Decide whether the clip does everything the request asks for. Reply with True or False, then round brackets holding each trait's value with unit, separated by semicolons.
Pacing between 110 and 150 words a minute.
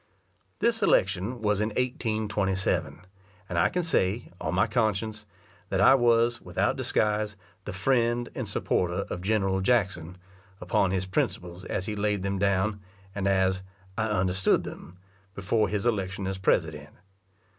True (145 wpm)